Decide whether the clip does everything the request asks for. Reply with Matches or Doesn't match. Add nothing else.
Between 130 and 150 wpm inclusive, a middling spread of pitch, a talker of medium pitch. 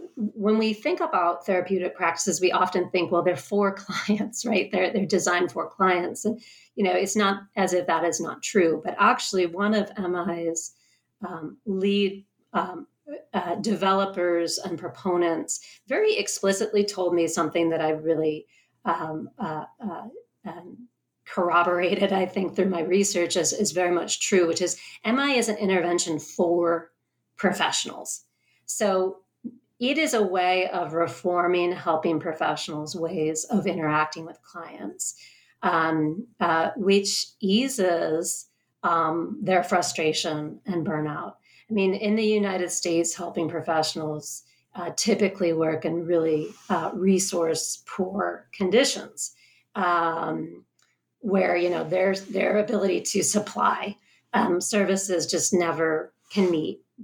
Matches